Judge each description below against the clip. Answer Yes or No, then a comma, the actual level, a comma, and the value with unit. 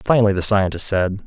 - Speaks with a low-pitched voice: Yes, low, 100 Hz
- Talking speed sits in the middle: Yes, average, 190 wpm